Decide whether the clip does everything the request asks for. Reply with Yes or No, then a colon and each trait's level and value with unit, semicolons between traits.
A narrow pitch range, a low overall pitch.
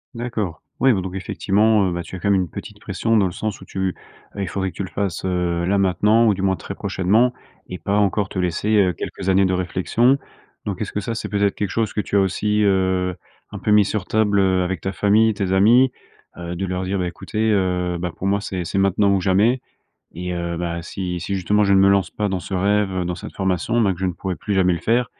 Yes: narrow, 2.3 semitones; very low, 95 Hz